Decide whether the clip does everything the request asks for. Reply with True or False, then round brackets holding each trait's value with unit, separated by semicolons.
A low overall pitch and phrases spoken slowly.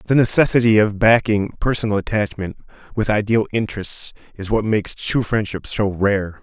False (105 Hz; 150 wpm)